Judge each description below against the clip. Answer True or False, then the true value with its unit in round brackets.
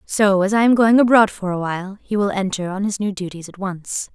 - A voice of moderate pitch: False (200 Hz)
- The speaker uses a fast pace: True (260 wpm)